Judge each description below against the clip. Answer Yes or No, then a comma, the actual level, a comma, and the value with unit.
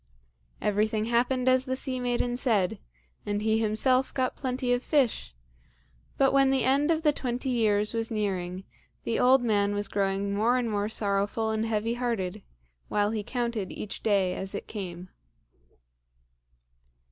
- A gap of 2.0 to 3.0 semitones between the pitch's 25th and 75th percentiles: No, average, 3.6 semitones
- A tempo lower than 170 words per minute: Yes, average, 155 wpm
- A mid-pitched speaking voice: No, high, 225 Hz